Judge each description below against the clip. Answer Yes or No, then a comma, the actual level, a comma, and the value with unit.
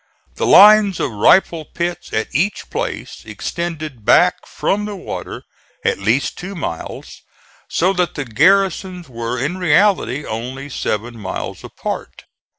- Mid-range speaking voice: Yes, medium, 160 Hz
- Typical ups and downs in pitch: No, wide, 7.4 semitones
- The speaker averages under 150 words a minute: Yes, slow, 135 wpm